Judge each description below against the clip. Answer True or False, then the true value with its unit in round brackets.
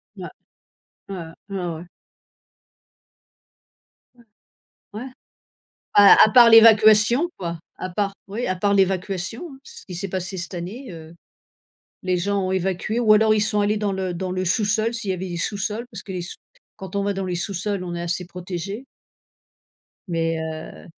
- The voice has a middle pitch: False (195 Hz)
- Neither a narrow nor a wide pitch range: True (3.0 semitones)